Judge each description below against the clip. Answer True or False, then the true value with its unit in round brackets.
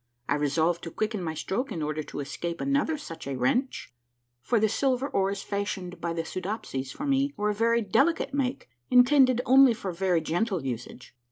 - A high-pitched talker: True (200 Hz)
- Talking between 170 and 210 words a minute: True (190 wpm)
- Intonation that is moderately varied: False (7.4 semitones)